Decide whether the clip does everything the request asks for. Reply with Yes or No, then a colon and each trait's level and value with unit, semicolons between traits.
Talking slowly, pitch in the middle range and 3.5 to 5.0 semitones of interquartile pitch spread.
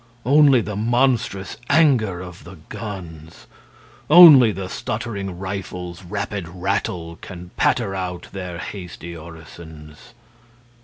No: slow, 105 wpm; very low, 95 Hz; average, 4.3 semitones